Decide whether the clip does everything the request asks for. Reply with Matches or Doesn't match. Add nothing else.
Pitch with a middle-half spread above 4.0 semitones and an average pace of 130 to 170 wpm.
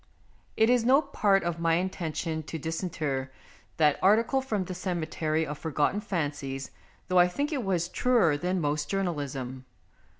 Matches